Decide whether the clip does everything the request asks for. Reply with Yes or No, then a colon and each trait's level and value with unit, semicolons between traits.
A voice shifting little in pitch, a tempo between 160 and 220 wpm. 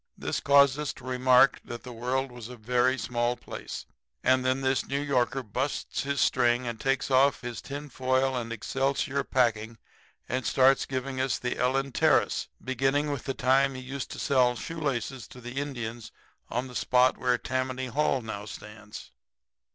Yes: narrow, 1.8 semitones; average, 175 wpm